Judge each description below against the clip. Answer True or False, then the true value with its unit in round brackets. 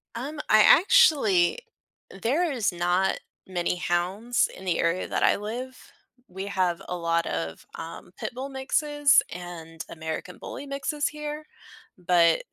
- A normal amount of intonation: False (7.9 semitones)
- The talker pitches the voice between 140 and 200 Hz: True (190 Hz)